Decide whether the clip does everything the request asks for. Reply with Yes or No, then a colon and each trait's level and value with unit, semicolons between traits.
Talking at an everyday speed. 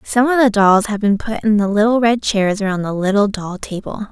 No: fast, 250 wpm